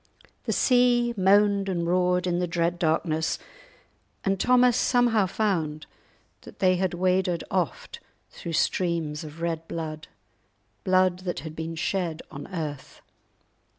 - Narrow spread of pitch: No, average, 3.0 semitones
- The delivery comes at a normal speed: No, slow, 120 wpm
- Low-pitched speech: No, medium, 180 Hz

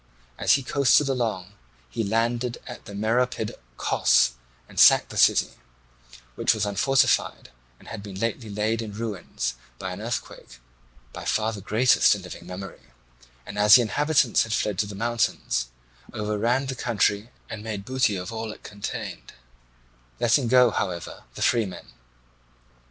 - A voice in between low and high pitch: No, low, 110 Hz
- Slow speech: No, average, 155 wpm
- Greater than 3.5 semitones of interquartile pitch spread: No, average, 3.0 semitones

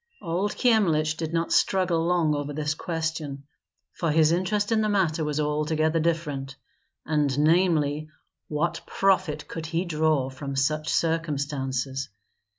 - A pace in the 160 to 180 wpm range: No, slow, 135 wpm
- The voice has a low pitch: No, medium, 155 Hz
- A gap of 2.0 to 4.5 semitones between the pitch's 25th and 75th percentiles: Yes, narrow, 2.4 semitones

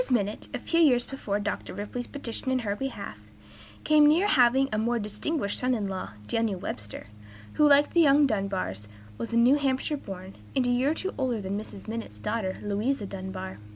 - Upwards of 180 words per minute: Yes, average, 190 wpm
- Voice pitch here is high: Yes, high, 230 Hz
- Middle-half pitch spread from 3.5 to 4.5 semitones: No, average, 5.3 semitones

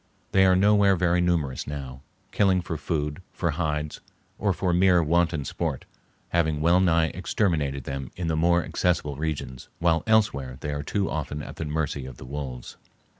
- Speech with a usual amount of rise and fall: Yes, average, 3.6 semitones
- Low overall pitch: Yes, very low, 80 Hz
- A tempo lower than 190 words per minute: Yes, average, 175 wpm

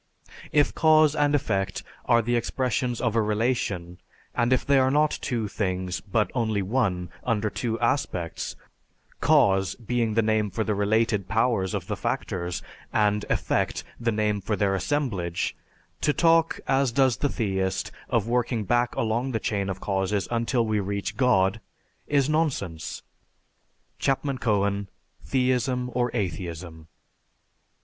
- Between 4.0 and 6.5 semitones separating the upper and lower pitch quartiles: Yes, average, 4.4 semitones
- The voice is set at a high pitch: No, low, 110 Hz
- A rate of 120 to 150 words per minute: Yes, average, 140 wpm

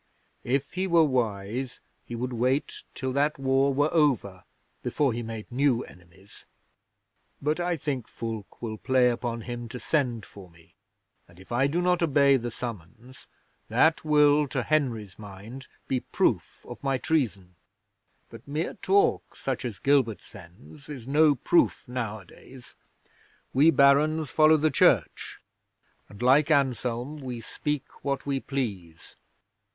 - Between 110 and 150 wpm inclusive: Yes, average, 145 wpm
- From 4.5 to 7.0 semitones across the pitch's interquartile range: No, average, 4.1 semitones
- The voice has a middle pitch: No, low, 130 Hz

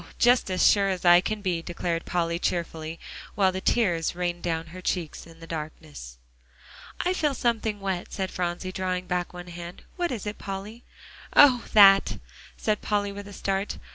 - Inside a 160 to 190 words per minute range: Yes, average, 175 wpm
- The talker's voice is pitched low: No, medium, 185 Hz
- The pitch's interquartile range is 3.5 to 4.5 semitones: No, average, 3.0 semitones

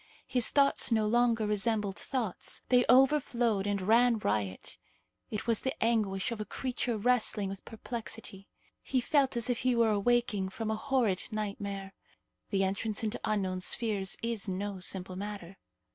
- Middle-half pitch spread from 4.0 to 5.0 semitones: No, average, 3.4 semitones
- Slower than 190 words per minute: Yes, average, 155 wpm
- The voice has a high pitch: Yes, high, 215 Hz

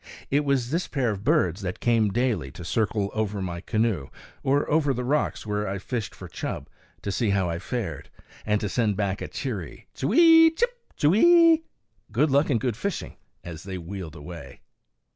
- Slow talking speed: No, average, 180 wpm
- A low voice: Yes, low, 110 Hz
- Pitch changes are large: Yes, wide, 6.7 semitones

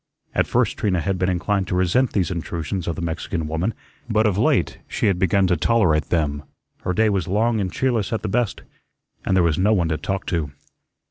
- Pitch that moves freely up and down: No, average, 3.7 semitones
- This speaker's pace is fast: Yes, fast, 215 wpm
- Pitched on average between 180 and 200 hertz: No, very low, 95 Hz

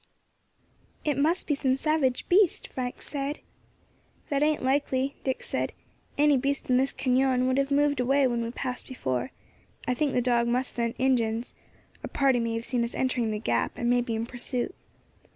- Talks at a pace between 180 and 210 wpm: Yes, average, 185 wpm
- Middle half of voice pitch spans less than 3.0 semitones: Yes, narrow, 2.5 semitones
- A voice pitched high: Yes, very high, 260 Hz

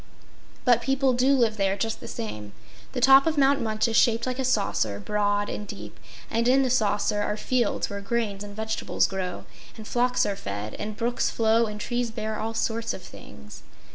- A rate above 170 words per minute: Yes, average, 200 wpm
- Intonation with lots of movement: No, average, 3.1 semitones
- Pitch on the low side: No, high, 220 Hz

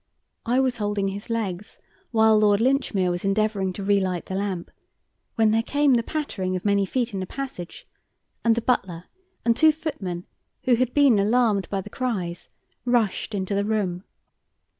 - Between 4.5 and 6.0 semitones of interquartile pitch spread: No, average, 3.9 semitones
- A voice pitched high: Yes, high, 210 Hz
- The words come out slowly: No, average, 170 wpm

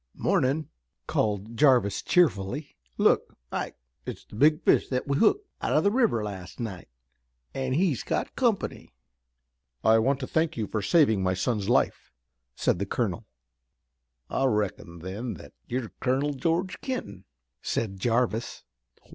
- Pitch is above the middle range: No, low, 120 Hz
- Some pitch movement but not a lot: No, wide, 6.5 semitones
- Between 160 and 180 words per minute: No, average, 145 wpm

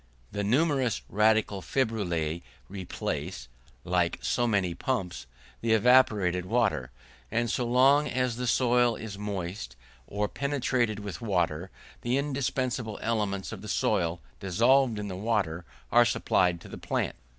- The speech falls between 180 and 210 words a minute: No, slow, 135 wpm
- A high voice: No, low, 105 Hz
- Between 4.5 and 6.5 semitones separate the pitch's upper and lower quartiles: Yes, average, 5.1 semitones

